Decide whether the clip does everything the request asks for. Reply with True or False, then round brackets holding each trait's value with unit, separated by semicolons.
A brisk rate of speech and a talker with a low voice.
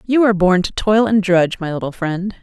False (245 wpm; 195 Hz)